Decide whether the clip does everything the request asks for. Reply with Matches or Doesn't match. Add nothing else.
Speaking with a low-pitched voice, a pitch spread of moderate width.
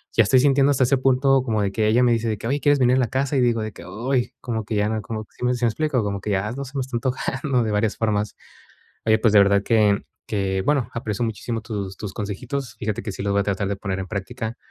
Matches